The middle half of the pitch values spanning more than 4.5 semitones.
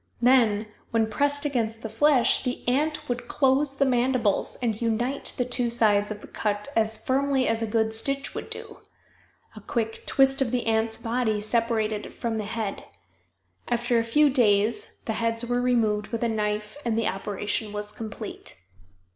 No: narrow, 2.6 semitones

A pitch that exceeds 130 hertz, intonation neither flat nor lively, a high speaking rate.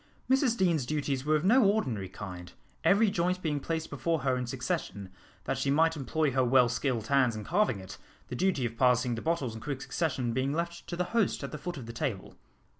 No: medium, 140 Hz; wide, 5.7 semitones; fast, 220 wpm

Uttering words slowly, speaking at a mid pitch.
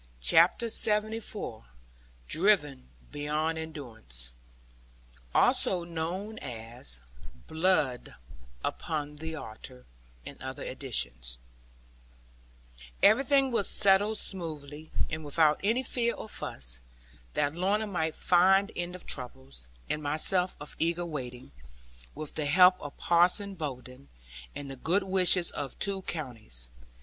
Yes: slow, 110 wpm; medium, 160 Hz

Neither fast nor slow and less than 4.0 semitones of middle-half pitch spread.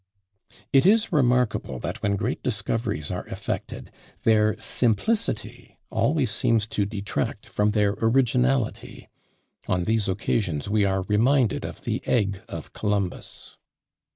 No: slow, 125 wpm; average, 3.6 semitones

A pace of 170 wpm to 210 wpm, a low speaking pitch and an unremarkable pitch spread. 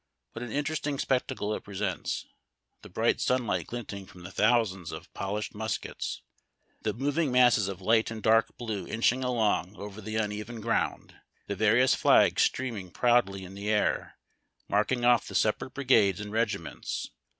No: average, 160 wpm; low, 110 Hz; average, 3.3 semitones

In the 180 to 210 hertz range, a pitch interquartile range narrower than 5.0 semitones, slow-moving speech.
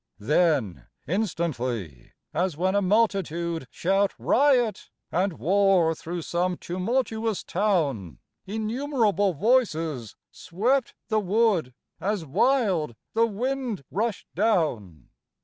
No: high, 190 Hz; average, 5.3 semitones; slow, 95 wpm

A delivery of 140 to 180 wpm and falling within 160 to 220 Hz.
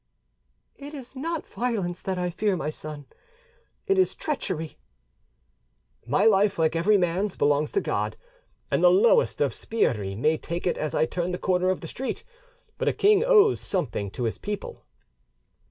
Yes: average, 170 wpm; medium, 185 Hz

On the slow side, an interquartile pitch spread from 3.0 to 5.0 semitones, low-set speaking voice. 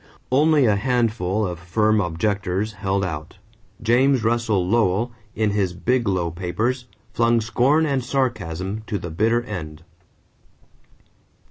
Yes: slow, 120 wpm; average, 4.5 semitones; low, 105 Hz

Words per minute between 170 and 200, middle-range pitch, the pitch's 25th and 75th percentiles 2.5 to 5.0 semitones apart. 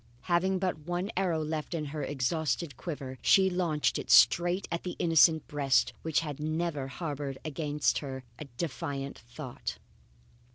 No: average, 150 wpm; medium, 155 Hz; average, 3.5 semitones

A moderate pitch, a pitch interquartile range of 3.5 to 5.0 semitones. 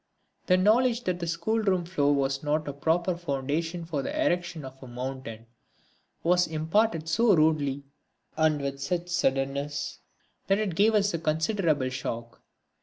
Yes: medium, 160 Hz; average, 4.5 semitones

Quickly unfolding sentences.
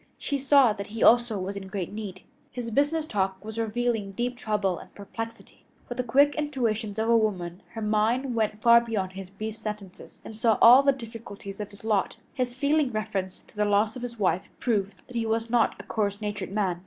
Yes: fast, 210 wpm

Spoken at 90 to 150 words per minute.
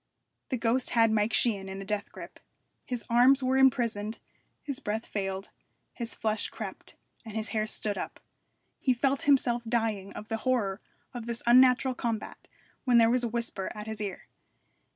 No: average, 170 wpm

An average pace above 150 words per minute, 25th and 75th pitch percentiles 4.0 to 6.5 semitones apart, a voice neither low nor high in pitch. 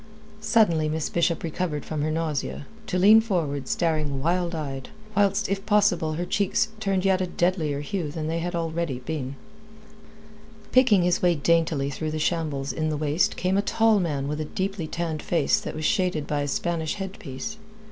No: average, 180 wpm; average, 3.6 semitones; medium, 165 Hz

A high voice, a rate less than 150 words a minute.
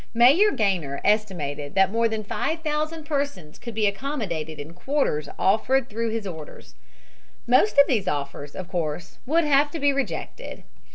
No: high, 220 Hz; average, 155 wpm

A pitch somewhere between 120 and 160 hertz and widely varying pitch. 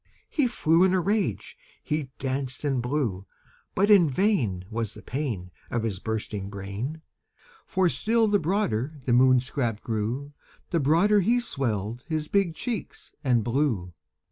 Yes: medium, 140 Hz; wide, 8.0 semitones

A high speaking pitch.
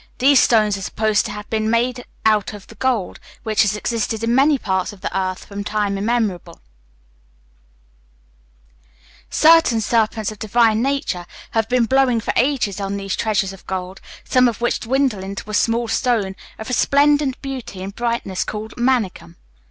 Yes: high, 220 Hz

